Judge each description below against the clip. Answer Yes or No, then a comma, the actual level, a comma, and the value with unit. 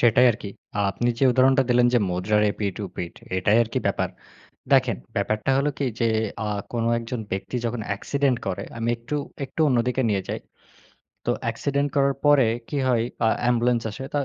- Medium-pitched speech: No, low, 120 Hz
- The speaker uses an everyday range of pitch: Yes, average, 3.7 semitones